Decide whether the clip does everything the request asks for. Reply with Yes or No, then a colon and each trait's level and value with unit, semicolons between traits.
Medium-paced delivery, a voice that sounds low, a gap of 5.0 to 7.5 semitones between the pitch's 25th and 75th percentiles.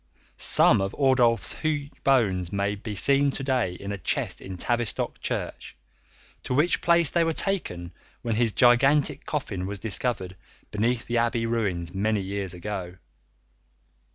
Yes: average, 150 wpm; low, 115 Hz; wide, 5.6 semitones